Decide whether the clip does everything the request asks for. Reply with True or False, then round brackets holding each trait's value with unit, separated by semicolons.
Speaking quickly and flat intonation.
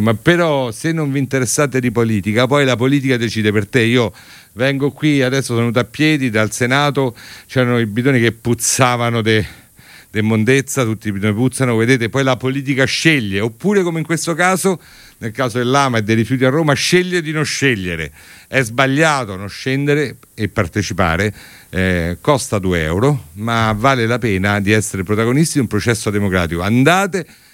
False (175 wpm; 4.5 semitones)